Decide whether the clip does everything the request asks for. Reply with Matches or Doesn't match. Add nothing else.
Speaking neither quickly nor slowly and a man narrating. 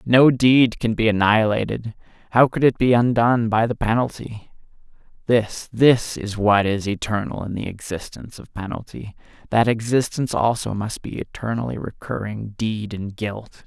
Matches